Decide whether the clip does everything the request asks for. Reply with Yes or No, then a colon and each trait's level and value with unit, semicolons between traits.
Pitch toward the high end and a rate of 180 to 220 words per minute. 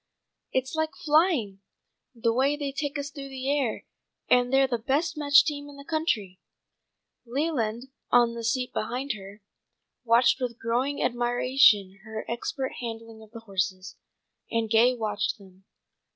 No: high, 245 Hz; average, 150 wpm